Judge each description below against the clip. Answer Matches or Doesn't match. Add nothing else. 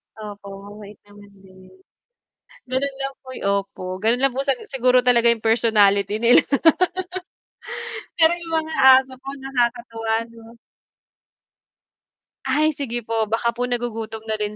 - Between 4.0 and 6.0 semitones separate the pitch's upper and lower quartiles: Doesn't match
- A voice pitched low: Doesn't match